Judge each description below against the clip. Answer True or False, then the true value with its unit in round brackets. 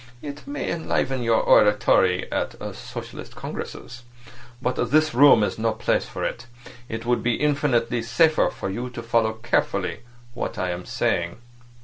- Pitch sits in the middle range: False (120 Hz)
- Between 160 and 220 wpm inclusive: False (150 wpm)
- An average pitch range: True (4.0 semitones)